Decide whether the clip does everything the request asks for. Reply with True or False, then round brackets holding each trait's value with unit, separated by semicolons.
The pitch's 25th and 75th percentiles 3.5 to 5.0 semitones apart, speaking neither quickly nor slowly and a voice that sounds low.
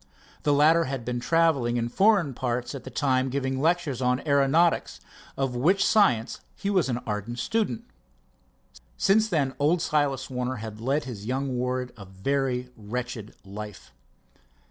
True (4.1 semitones; 150 wpm; 130 Hz)